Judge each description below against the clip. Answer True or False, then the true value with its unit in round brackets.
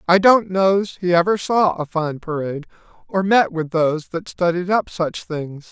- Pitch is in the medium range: True (175 Hz)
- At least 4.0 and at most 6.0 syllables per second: True (4.5 syllables/s)